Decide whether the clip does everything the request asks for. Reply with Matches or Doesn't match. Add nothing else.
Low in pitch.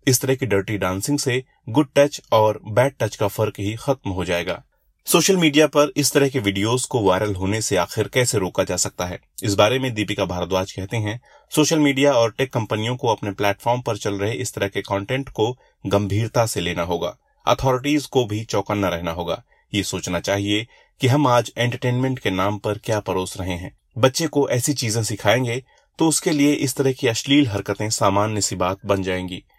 Matches